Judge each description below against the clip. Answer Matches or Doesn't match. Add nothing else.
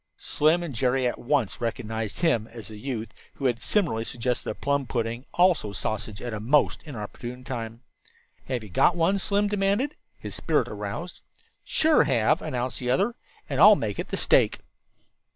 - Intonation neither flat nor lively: Doesn't match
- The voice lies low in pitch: Matches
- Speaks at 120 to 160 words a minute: Doesn't match